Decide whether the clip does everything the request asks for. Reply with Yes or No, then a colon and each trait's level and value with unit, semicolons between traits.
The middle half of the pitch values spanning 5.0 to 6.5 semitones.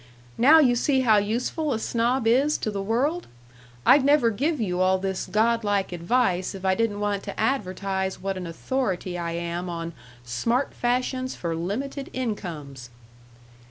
Yes: wide, 5.5 semitones